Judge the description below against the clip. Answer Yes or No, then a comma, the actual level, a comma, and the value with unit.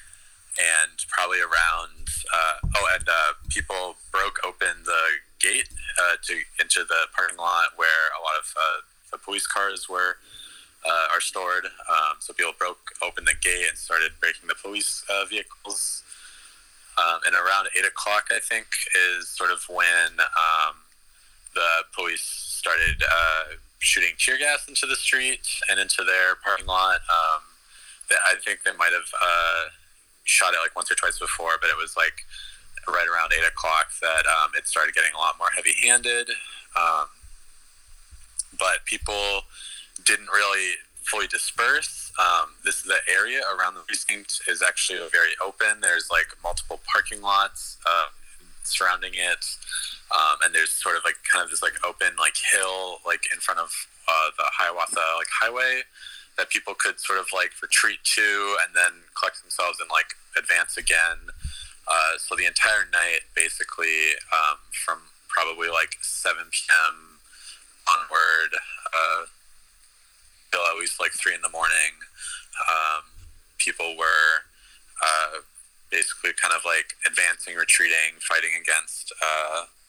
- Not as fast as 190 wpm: Yes, average, 150 wpm